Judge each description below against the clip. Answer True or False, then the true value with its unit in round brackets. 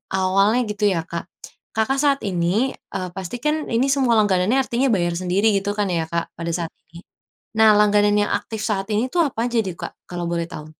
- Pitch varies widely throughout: False (4.1 semitones)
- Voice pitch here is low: False (200 Hz)